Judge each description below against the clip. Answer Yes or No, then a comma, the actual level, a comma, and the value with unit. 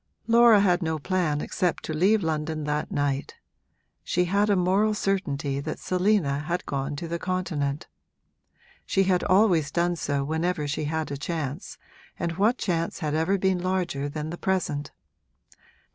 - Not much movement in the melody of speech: No, average, 3.9 semitones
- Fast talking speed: No, average, 160 wpm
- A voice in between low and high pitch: Yes, medium, 170 Hz